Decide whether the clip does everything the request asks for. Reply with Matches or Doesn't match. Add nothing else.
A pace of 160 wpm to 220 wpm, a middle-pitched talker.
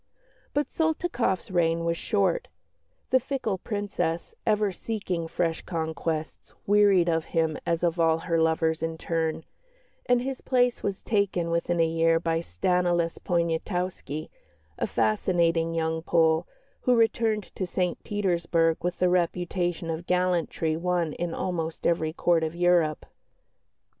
Doesn't match